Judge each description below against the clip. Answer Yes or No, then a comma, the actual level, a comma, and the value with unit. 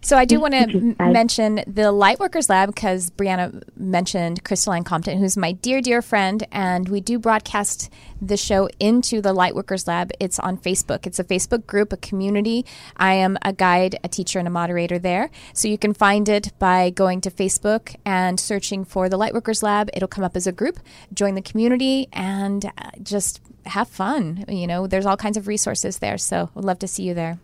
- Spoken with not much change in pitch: Yes, narrow, 2.3 semitones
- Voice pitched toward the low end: No, high, 195 Hz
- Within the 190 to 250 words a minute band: Yes, average, 200 wpm